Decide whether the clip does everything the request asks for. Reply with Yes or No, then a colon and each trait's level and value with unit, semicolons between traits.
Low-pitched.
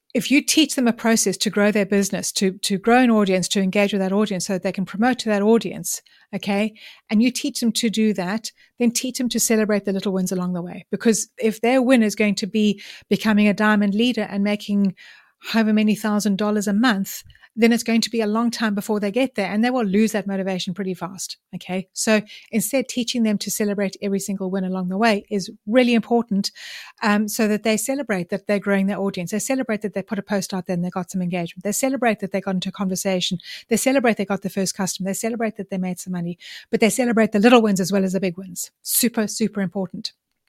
No: high, 210 Hz